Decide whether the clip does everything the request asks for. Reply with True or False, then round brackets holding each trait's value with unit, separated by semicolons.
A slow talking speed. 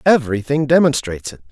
True (120 wpm)